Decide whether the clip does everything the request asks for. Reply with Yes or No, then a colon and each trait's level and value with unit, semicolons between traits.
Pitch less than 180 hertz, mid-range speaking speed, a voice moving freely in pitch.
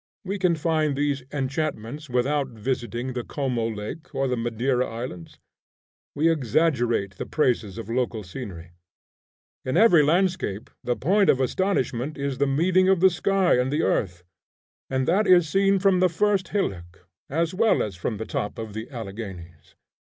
Yes: low, 135 Hz; average, 160 wpm; wide, 6.7 semitones